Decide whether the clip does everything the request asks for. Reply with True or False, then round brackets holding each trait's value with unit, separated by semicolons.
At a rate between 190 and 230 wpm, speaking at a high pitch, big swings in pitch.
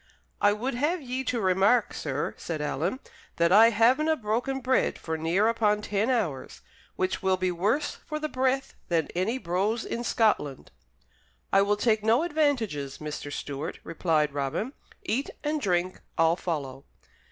False (155 wpm; 210 Hz; 6.8 semitones)